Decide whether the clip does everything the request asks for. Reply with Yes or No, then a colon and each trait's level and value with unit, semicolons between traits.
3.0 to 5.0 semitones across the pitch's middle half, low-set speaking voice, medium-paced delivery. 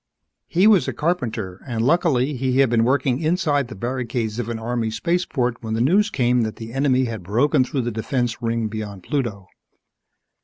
Yes: average, 3.8 semitones; low, 125 Hz; average, 190 wpm